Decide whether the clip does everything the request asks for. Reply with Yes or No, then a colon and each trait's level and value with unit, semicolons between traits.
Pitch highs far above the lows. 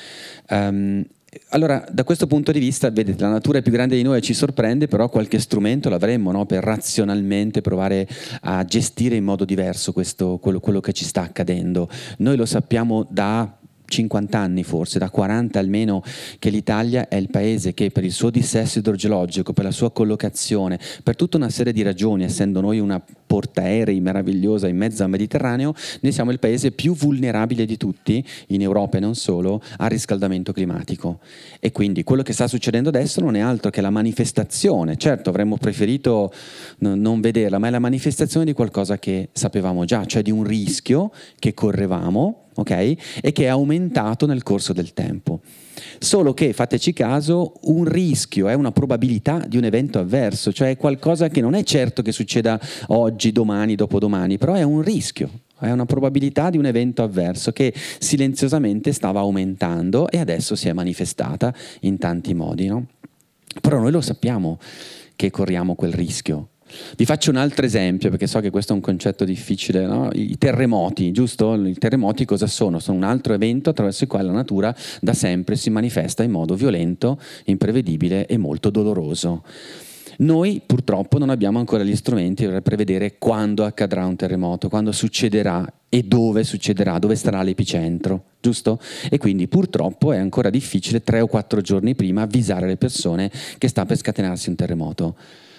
No: average, 4.2 semitones